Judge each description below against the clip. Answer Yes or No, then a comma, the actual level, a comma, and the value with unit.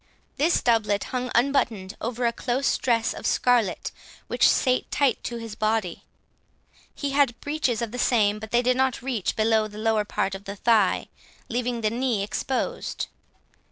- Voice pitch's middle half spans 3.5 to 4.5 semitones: No, average, 2.8 semitones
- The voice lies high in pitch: Yes, high, 235 Hz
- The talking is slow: No, average, 165 wpm